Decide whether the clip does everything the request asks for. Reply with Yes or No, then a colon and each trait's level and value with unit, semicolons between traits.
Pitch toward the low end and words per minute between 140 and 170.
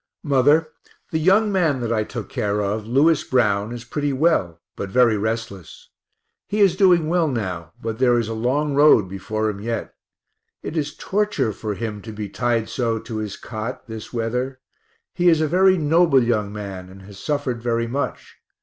No: low, 120 Hz; average, 185 wpm